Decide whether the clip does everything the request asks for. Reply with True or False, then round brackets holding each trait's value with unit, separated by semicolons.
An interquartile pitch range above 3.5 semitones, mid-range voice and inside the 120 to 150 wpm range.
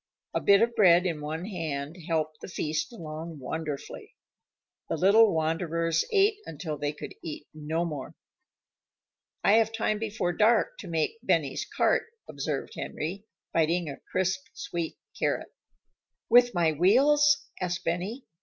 True (5.1 semitones; 170 Hz; 140 wpm)